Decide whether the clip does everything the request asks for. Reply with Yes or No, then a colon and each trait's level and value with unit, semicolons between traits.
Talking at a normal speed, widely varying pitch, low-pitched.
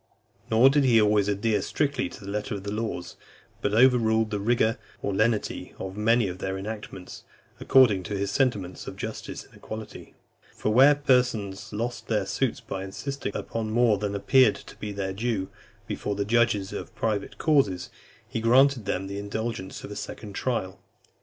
No: average, 175 wpm; average, 3.1 semitones; low, 110 Hz